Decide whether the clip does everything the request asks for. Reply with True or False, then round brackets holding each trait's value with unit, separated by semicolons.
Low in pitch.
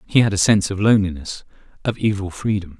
True (100 Hz)